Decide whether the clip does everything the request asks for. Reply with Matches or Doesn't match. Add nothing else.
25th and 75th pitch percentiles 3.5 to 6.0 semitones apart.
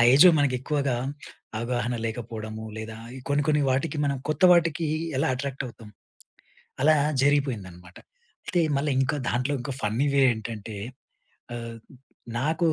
Matches